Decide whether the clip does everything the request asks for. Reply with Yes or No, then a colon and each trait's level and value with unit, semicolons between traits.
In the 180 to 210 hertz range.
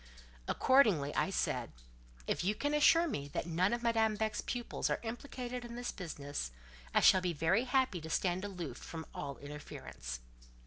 Yes: medium, 185 Hz